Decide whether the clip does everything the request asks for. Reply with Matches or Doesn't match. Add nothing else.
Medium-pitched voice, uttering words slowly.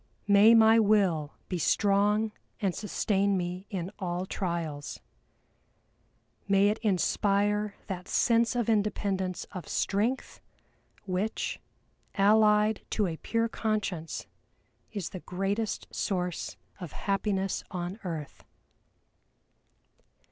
Doesn't match